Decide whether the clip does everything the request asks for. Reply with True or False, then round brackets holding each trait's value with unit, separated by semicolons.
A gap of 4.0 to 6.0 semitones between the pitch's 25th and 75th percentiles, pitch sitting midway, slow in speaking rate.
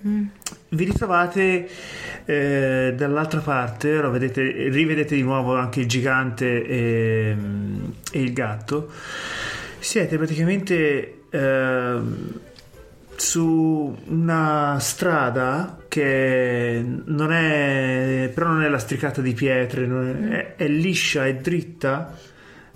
True (4.4 semitones; 145 Hz; 100 wpm)